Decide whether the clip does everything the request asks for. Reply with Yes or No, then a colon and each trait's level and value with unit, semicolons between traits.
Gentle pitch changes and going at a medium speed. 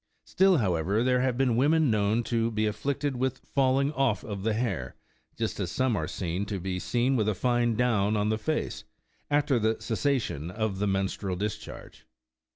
No: average, 4.2 semitones; average, 175 wpm